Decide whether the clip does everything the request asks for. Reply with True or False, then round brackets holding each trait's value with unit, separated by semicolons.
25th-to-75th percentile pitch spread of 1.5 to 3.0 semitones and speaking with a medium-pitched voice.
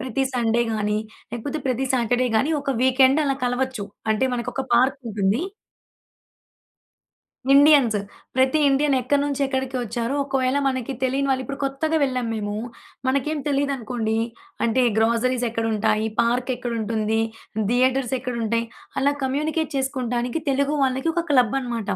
False (2.7 semitones; 255 Hz)